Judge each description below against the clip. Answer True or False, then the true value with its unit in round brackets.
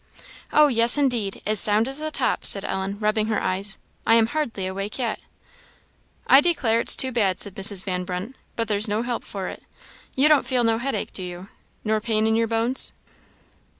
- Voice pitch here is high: True (220 Hz)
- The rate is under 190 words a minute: False (195 wpm)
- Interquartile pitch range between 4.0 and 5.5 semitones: False (3.5 semitones)